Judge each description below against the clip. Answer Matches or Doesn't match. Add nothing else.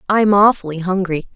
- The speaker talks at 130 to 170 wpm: Matches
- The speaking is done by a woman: Matches